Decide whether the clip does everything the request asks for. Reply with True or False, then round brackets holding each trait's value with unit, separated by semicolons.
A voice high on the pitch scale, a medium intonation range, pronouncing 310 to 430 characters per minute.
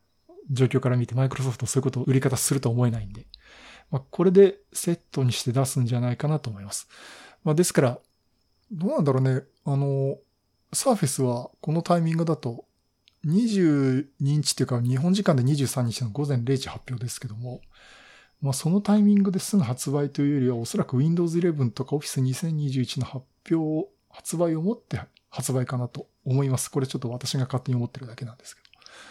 False (135 Hz; 4.3 semitones; 385 characters per minute)